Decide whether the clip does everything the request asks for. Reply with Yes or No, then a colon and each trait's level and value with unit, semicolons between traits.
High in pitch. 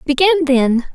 Yes: very high, 295 Hz